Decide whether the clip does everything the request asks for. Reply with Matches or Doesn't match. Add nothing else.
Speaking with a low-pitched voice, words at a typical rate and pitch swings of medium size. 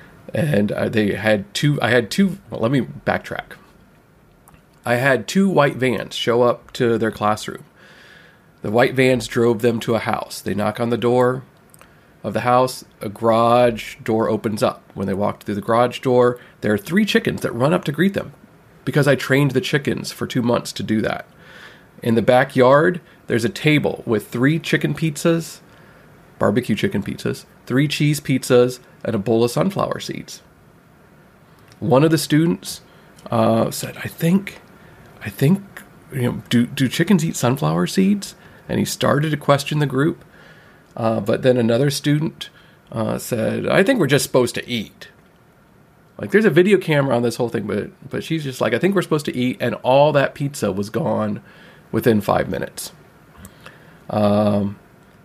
Doesn't match